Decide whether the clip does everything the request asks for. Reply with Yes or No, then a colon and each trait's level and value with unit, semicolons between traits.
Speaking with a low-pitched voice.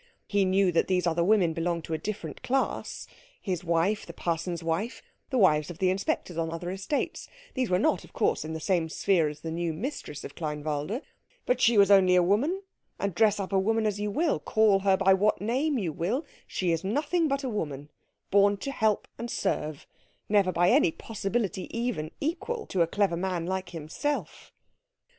No: high, 190 Hz